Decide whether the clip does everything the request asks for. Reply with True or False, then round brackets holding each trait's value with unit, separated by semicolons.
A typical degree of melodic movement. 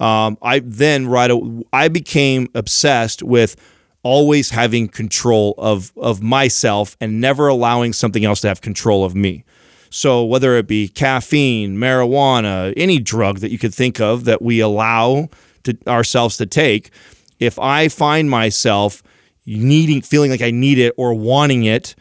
True (3.3 semitones)